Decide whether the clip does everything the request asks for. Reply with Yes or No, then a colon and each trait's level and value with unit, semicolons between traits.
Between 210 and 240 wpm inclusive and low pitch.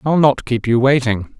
Yes: fast, 215 wpm; low, 125 Hz